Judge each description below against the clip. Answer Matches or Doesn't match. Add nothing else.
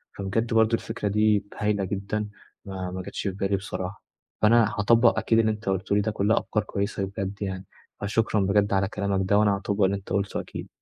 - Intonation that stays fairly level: Matches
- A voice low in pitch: Matches